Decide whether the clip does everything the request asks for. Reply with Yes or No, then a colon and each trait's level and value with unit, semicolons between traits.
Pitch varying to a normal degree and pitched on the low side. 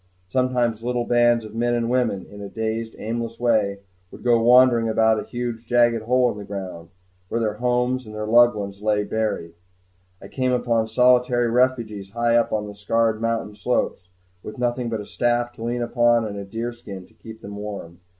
No: narrow, 2.3 semitones; low, 115 Hz